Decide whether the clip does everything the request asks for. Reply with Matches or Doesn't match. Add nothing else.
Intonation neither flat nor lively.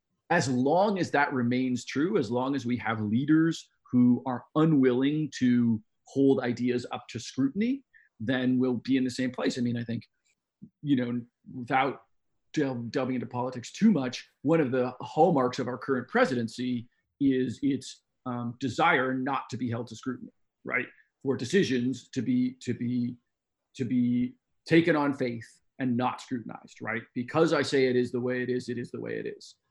Doesn't match